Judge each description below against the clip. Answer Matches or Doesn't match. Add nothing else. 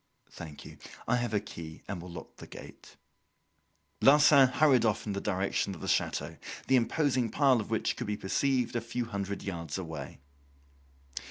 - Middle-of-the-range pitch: Doesn't match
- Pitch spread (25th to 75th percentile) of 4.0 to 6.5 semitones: Matches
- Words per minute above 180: Doesn't match